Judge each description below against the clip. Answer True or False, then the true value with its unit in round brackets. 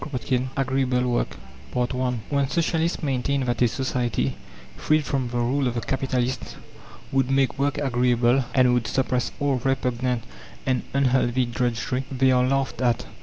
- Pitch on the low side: True (130 Hz)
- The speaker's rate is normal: True (155 wpm)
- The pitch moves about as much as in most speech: False (1.6 semitones)